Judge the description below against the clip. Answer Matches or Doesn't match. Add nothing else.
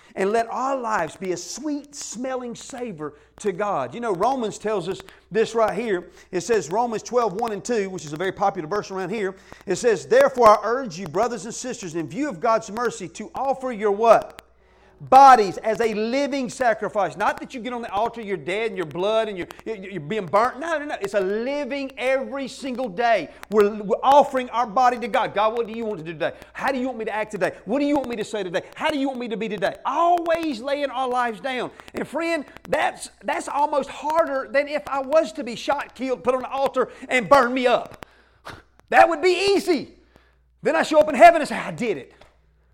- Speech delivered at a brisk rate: Matches